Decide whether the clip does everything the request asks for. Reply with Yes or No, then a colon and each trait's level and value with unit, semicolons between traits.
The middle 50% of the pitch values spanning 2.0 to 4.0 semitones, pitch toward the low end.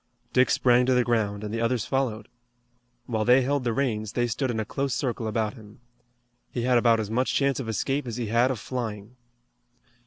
Yes: narrow, 2.6 semitones; low, 120 Hz